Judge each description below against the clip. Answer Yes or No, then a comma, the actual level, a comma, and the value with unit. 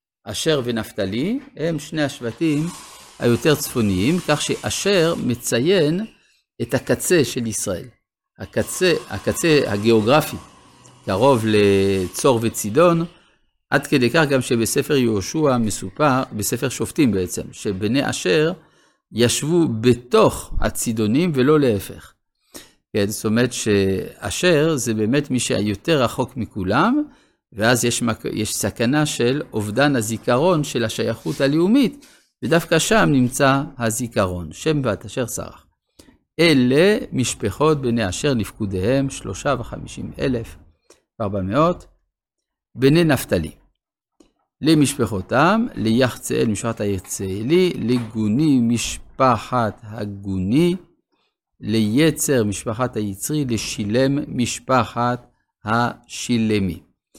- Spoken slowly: Yes, slow, 95 wpm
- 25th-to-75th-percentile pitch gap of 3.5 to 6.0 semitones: Yes, wide, 5.5 semitones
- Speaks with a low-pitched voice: Yes, low, 125 Hz